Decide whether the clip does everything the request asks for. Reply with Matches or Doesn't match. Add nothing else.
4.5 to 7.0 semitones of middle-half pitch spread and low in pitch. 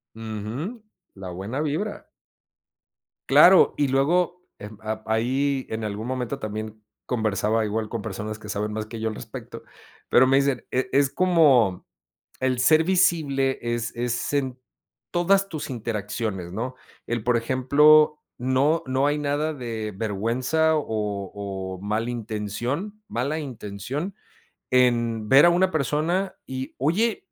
Matches